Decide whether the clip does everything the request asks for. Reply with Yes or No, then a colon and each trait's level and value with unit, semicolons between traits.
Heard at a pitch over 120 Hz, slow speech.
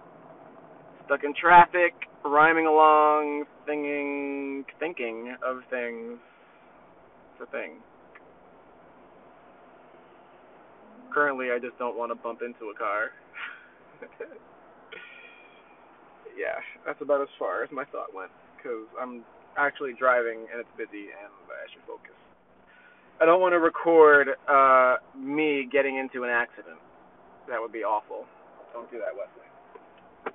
Yes: medium, 140 Hz; slow, 120 wpm